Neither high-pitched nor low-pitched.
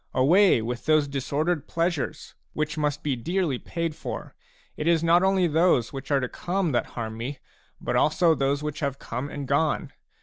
Yes: medium, 150 Hz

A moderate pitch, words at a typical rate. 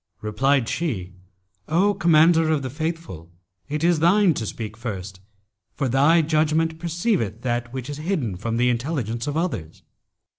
Yes: medium, 145 Hz; average, 150 wpm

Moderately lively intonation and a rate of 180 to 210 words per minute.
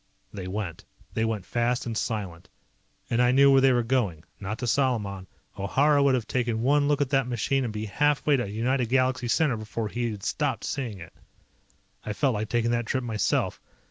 Yes: average, 3.5 semitones; fast, 205 wpm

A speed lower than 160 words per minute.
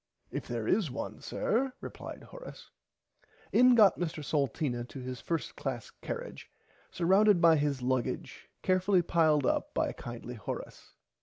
Yes: average, 140 wpm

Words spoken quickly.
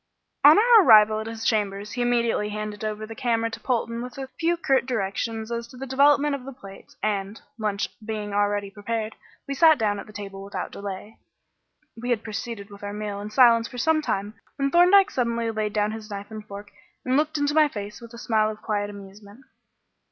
Yes: fast, 210 wpm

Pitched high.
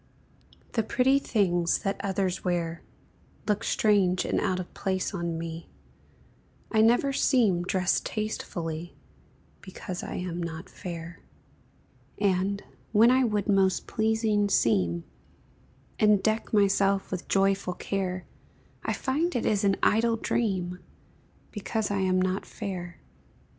Yes: high, 195 Hz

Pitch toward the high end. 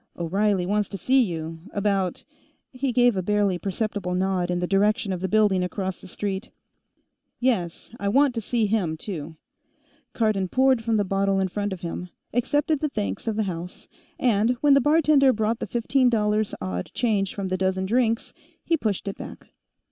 Yes: high, 205 Hz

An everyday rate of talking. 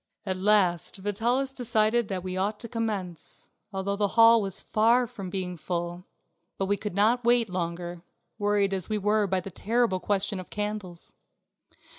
Yes: average, 165 wpm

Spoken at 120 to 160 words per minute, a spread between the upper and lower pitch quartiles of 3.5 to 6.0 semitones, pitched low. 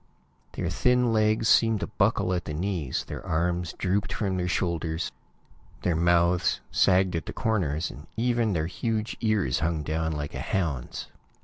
Yes: average, 155 wpm; average, 4.9 semitones; very low, 90 Hz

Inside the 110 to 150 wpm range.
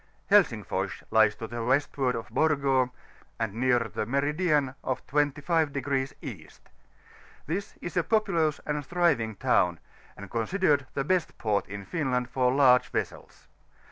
Yes: average, 140 wpm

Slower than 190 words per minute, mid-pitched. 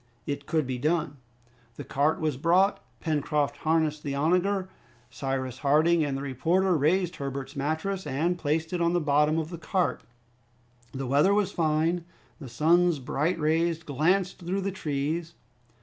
Yes: average, 155 wpm; medium, 155 Hz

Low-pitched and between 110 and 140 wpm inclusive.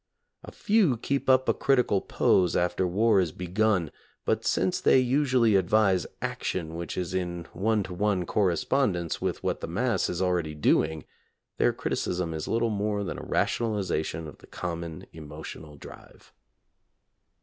No: very low, 95 Hz; average, 150 wpm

